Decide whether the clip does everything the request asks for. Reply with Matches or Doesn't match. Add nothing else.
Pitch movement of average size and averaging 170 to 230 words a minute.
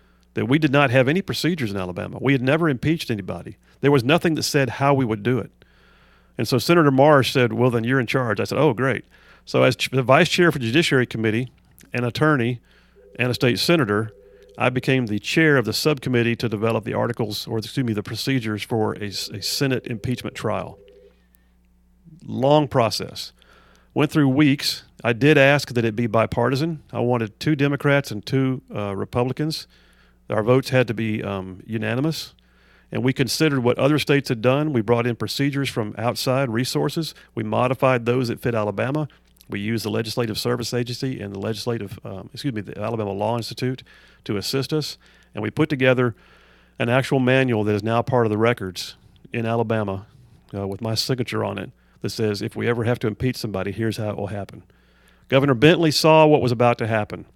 Matches